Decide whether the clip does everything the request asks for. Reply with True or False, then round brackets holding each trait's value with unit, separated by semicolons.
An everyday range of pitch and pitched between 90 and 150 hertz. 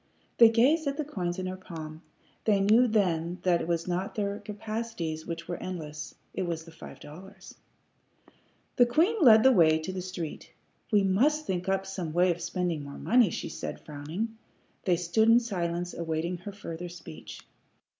False (4.5 semitones; 185 Hz)